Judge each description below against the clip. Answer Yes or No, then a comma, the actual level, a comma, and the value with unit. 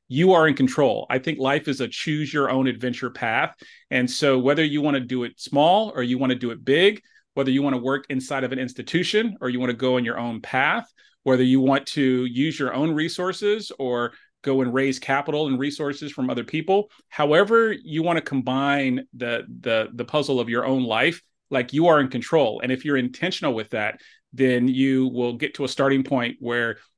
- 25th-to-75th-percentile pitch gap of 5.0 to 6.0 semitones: No, average, 2.9 semitones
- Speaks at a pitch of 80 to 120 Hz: No, low, 135 Hz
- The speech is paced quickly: Yes, fast, 220 wpm